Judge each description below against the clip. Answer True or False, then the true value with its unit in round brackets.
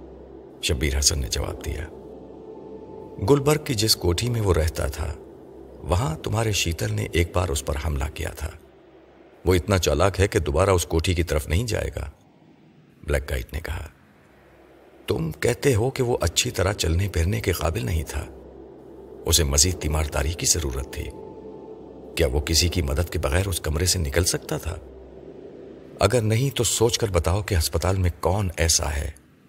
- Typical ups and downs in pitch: True (3.9 semitones)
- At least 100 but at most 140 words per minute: False (175 wpm)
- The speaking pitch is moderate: False (85 Hz)